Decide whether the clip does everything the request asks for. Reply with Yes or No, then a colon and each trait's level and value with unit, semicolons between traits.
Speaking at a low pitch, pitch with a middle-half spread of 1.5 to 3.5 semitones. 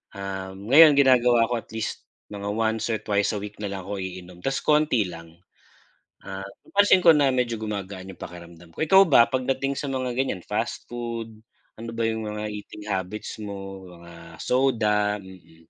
No: low, 105 Hz; average, 4.5 semitones